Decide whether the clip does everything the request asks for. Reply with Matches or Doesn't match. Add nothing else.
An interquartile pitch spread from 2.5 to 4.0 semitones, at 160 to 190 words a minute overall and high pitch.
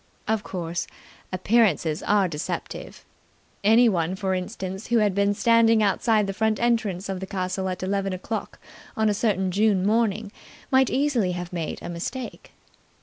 Doesn't match